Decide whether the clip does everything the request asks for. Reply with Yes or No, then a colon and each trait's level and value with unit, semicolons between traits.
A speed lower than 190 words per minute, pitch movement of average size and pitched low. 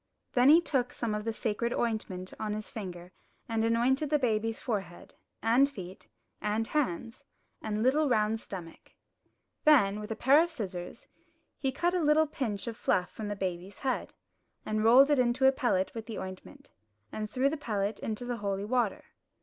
No: average, 180 wpm; average, 4.2 semitones; high, 225 Hz